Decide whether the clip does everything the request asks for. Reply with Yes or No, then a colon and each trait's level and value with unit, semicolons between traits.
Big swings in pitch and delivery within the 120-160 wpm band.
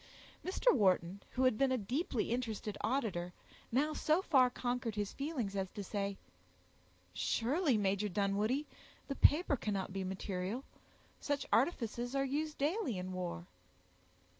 Yes: wide, 5.7 semitones; average, 140 wpm